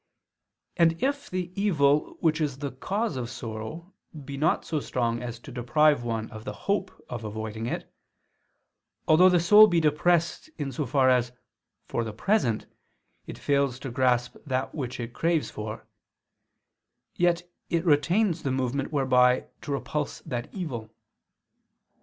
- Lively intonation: Yes, wide, 5.7 semitones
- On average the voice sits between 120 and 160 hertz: Yes, medium, 140 Hz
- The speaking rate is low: No, average, 150 wpm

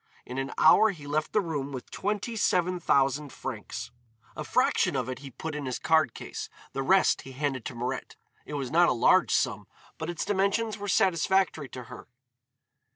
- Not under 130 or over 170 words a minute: No, average, 190 wpm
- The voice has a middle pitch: Yes, medium, 150 Hz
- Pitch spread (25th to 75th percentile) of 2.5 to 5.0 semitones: No, wide, 5.5 semitones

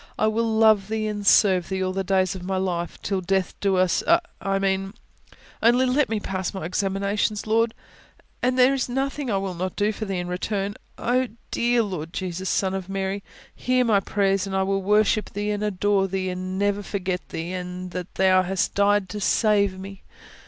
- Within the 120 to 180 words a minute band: No, average, 200 wpm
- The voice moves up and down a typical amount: No, narrow, 2.2 semitones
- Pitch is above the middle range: Yes, high, 195 Hz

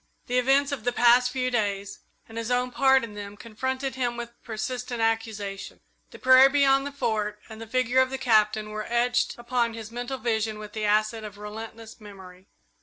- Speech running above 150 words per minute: Yes, average, 190 wpm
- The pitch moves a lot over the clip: No, average, 2.8 semitones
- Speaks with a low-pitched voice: No, high, 230 Hz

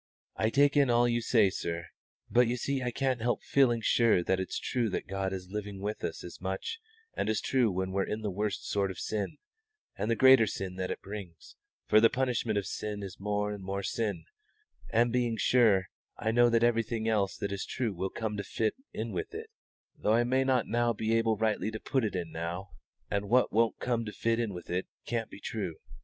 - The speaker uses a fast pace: Yes, fast, 225 wpm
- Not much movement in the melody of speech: No, average, 3.4 semitones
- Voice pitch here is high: No, low, 110 Hz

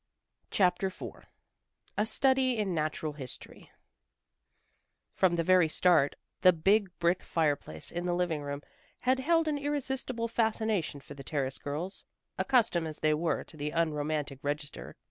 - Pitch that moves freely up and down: Yes, wide, 6.5 semitones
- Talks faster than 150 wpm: No, average, 145 wpm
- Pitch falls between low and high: Yes, medium, 175 Hz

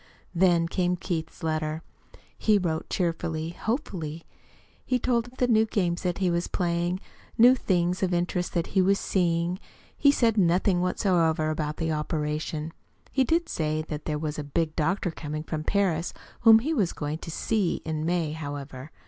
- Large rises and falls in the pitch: No, average, 3.5 semitones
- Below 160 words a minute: No, average, 165 wpm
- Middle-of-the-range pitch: Yes, medium, 170 Hz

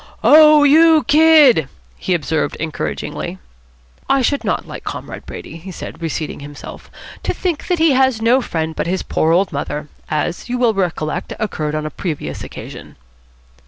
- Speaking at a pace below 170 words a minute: Yes, average, 160 wpm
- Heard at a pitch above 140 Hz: Yes, high, 190 Hz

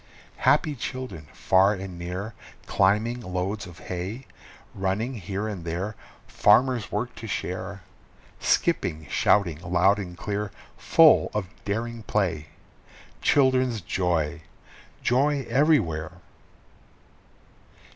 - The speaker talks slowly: Yes, slow, 100 wpm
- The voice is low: Yes, low, 100 Hz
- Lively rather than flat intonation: No, average, 4.7 semitones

